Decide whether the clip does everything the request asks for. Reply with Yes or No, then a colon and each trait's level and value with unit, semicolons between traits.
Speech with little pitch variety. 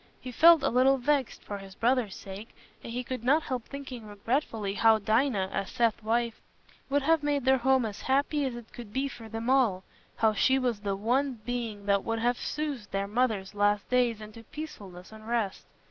No: average, 4.0 semitones